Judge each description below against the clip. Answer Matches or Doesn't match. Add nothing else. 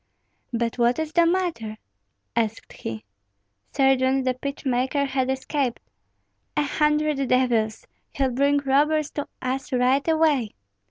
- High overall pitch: Matches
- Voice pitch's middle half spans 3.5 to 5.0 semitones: Doesn't match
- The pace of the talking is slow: Matches